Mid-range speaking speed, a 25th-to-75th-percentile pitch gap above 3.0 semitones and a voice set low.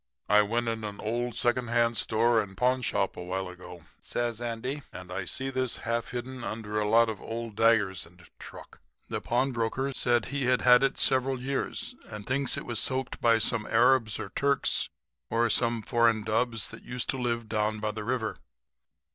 No: average, 185 wpm; narrow, 2.6 semitones; low, 115 Hz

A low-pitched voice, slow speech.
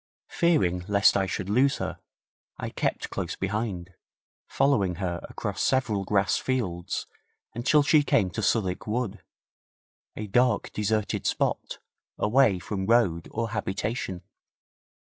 Yes: low, 105 Hz; slow, 125 wpm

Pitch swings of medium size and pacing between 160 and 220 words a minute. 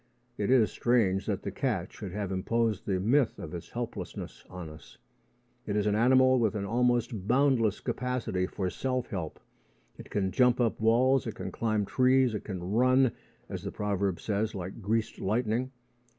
Yes: average, 4.1 semitones; average, 175 wpm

